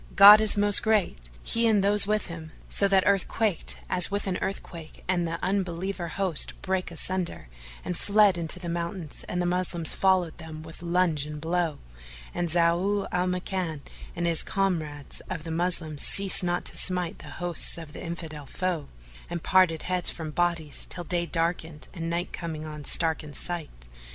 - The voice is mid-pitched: Yes, medium, 175 Hz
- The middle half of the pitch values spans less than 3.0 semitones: Yes, narrow, 2.5 semitones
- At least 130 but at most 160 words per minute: No, average, 175 wpm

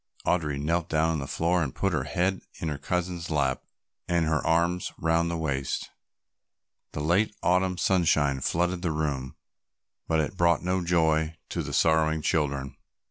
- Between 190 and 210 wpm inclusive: No, average, 165 wpm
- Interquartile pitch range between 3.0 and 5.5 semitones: No, narrow, 2.5 semitones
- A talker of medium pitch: No, very low, 80 Hz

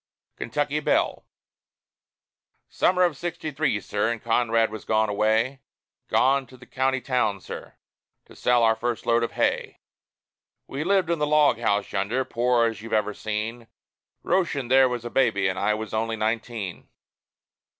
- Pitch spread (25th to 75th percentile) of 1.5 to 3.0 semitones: No, average, 3.5 semitones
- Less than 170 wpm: Yes, average, 160 wpm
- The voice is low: Yes, low, 120 Hz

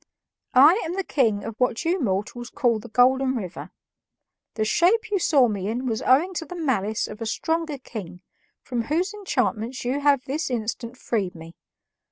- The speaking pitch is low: No, very high, 250 Hz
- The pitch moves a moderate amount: No, wide, 6.2 semitones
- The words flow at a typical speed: Yes, average, 180 wpm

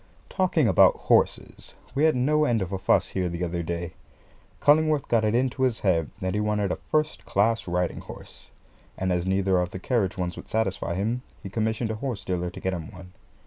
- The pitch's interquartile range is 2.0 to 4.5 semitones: No, average, 5.1 semitones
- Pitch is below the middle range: Yes, low, 100 Hz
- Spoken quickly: Yes, fast, 210 wpm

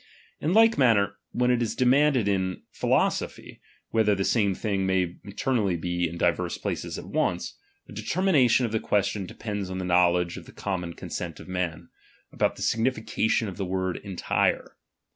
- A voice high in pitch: No, low, 100 Hz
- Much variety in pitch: No, average, 4.2 semitones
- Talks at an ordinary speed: Yes, average, 180 wpm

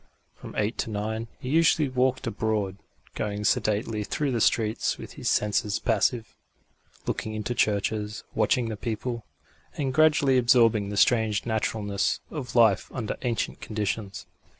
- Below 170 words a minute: Yes, average, 140 wpm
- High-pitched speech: No, low, 110 Hz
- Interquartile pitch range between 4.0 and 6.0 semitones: No, average, 2.9 semitones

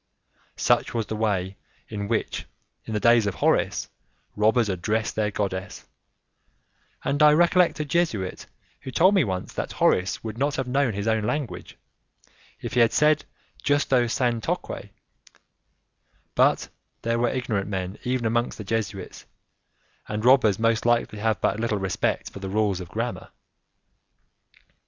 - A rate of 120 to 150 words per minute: Yes, average, 145 wpm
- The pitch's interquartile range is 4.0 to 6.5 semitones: No, average, 3.5 semitones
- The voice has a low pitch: Yes, low, 110 Hz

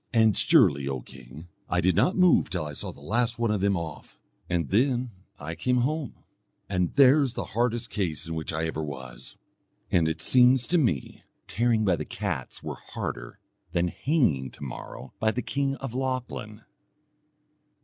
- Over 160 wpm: Yes, average, 180 wpm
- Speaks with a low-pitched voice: Yes, low, 105 Hz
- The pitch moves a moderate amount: No, wide, 7.6 semitones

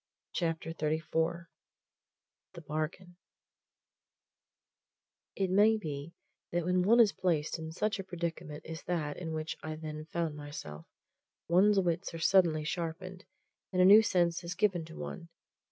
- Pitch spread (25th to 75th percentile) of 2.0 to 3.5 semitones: Yes, average, 2.7 semitones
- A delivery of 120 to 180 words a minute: Yes, average, 140 wpm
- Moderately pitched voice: Yes, medium, 170 Hz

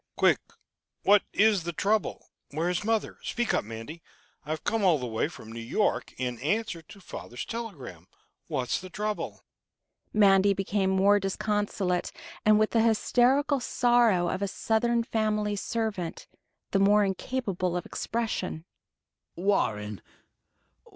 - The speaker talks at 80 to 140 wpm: Yes, slow, 135 wpm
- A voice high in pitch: Yes, high, 200 Hz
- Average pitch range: Yes, average, 4.3 semitones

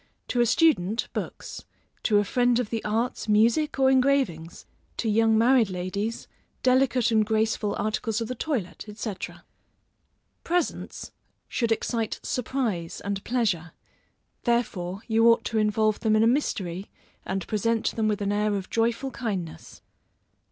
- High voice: Yes, high, 220 Hz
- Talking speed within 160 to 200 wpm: No, average, 145 wpm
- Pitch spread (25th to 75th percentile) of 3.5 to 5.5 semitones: No, average, 2.8 semitones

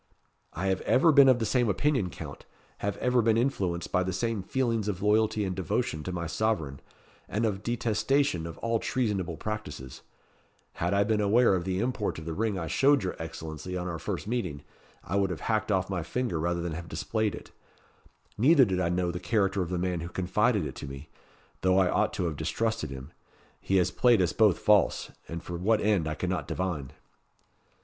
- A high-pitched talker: No, very low, 95 Hz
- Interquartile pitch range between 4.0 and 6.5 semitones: Yes, average, 4.5 semitones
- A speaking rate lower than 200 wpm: No, fast, 205 wpm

